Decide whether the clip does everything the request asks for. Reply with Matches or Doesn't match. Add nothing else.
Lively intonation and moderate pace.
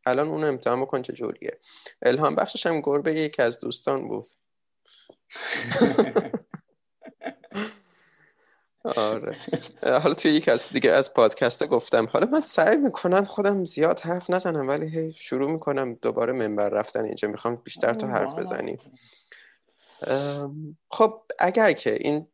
Matches